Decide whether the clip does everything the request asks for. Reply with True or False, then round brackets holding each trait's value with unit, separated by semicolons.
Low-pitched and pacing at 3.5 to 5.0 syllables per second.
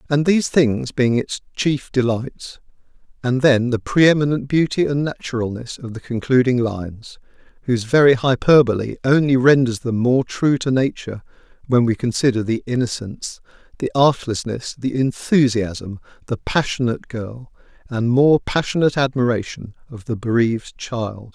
True (125 Hz; 4.9 syllables/s)